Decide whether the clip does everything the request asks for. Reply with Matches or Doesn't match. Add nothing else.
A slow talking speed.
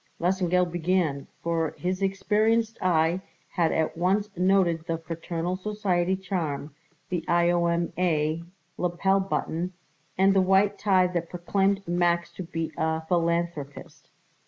Matches